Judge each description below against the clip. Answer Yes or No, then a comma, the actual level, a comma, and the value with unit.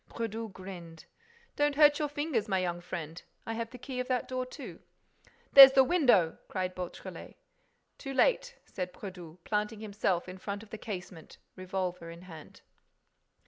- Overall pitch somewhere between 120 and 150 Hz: No, high, 205 Hz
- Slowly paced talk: No, average, 160 wpm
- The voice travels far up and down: Yes, wide, 5.9 semitones